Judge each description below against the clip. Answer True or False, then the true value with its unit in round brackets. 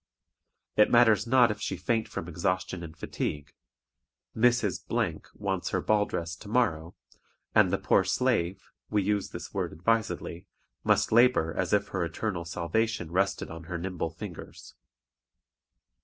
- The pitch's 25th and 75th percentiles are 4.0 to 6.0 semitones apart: True (4.5 semitones)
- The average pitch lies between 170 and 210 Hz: False (95 Hz)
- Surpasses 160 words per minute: False (140 wpm)